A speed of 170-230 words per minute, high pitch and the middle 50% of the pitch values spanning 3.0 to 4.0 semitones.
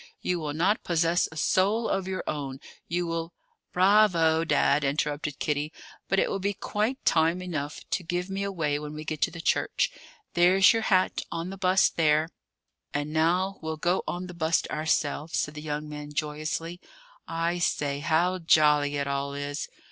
No: average, 180 wpm; medium, 165 Hz; average, 3.3 semitones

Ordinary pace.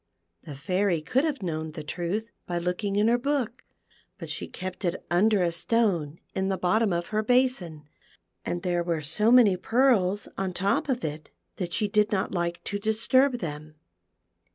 Yes: average, 180 wpm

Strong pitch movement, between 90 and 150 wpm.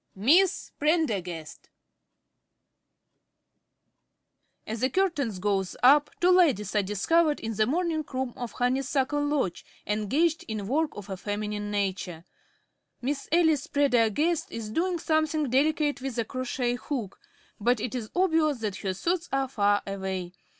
Yes: wide, 6.8 semitones; slow, 135 wpm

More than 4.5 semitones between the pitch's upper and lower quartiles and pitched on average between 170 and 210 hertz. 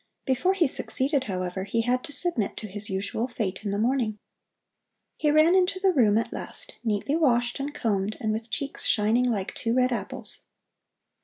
No: average, 5.2 semitones; high, 240 Hz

